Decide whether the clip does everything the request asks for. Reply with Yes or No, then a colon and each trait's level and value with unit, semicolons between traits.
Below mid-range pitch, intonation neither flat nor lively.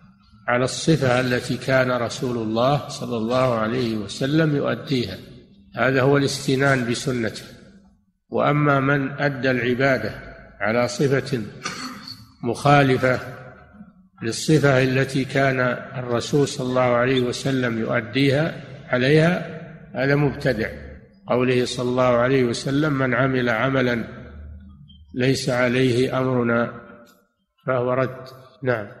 No: low, 130 Hz; narrow, 2.2 semitones